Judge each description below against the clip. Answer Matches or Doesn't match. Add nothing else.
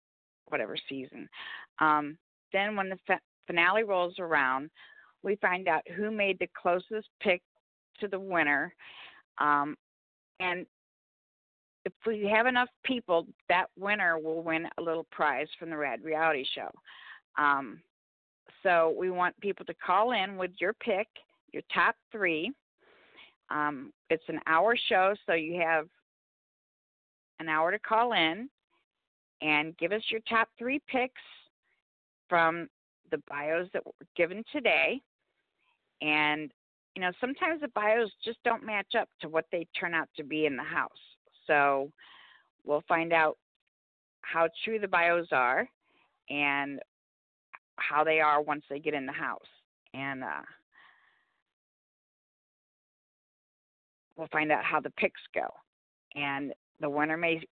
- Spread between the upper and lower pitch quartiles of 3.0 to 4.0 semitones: Doesn't match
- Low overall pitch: Doesn't match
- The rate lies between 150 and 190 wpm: Doesn't match